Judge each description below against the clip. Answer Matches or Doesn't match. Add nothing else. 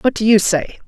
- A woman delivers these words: Matches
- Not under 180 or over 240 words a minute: Doesn't match